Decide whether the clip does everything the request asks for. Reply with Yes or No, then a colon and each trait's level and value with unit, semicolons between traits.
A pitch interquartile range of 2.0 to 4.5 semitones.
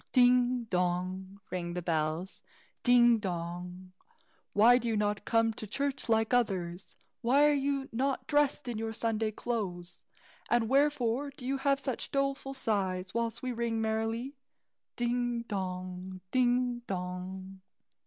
No: average, 5.0 semitones